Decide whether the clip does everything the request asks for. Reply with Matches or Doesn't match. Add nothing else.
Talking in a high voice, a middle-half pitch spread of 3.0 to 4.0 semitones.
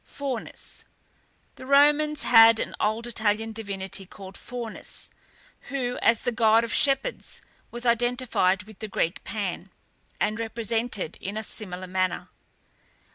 Matches